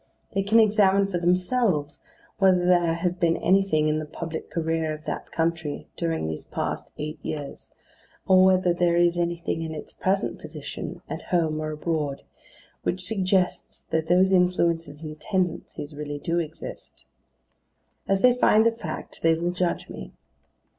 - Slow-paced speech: No, average, 155 wpm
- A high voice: No, medium, 170 Hz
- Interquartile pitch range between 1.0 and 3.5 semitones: Yes, average, 2.9 semitones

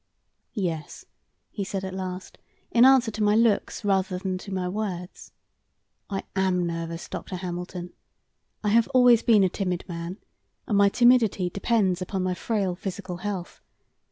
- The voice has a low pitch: No, high, 190 Hz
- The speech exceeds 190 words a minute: No, average, 155 wpm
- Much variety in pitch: No, narrow, 2.6 semitones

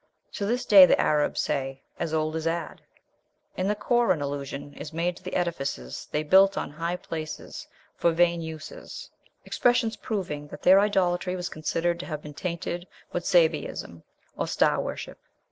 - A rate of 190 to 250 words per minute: No, average, 165 wpm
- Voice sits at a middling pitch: Yes, medium, 170 Hz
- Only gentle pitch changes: No, average, 3.3 semitones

